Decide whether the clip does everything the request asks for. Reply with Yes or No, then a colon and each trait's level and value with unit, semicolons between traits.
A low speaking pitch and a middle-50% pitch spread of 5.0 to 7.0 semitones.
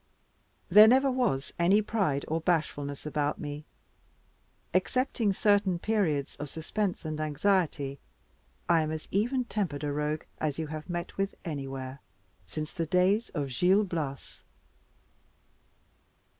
No: medium, 165 Hz; average, 5.3 semitones